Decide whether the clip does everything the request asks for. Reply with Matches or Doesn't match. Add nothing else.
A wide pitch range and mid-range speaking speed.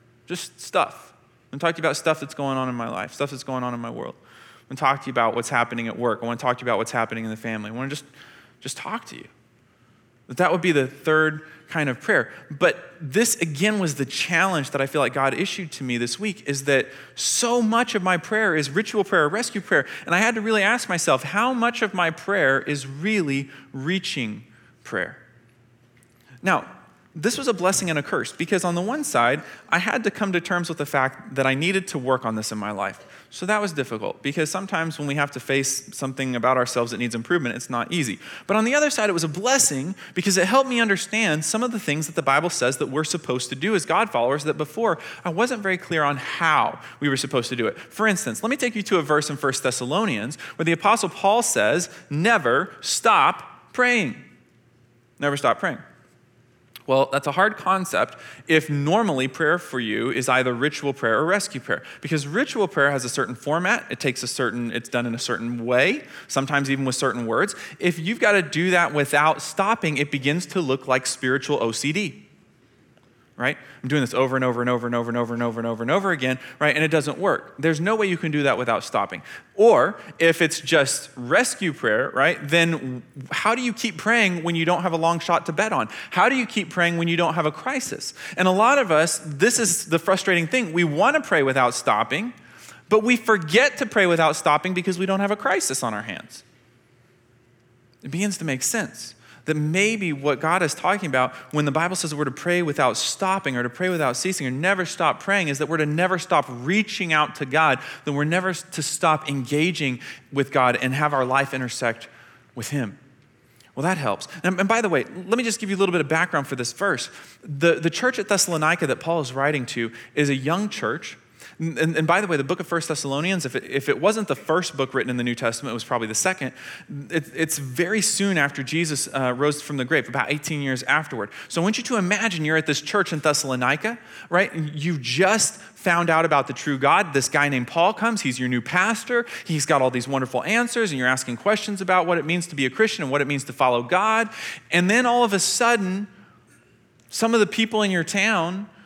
Doesn't match